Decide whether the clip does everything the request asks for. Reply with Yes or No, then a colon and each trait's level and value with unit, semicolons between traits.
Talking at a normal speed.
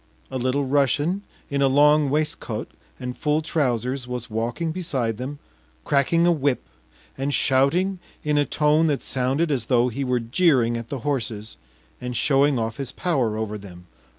Yes: average, 165 wpm